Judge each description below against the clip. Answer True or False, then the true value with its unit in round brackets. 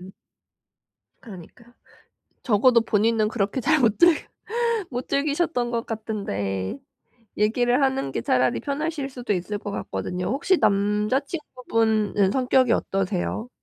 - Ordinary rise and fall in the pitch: True (4.5 semitones)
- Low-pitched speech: False (225 Hz)